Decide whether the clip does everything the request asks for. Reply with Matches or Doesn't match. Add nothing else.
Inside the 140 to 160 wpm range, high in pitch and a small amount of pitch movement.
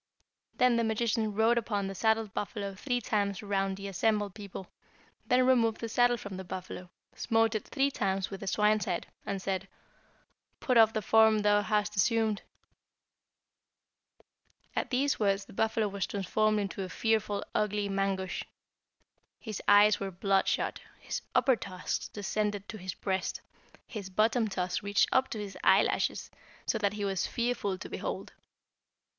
Matches